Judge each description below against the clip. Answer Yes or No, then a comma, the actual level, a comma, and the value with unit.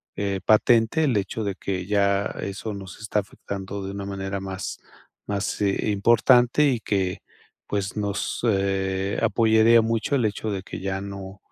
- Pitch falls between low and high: No, low, 100 Hz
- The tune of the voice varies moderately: No, narrow, 2.2 semitones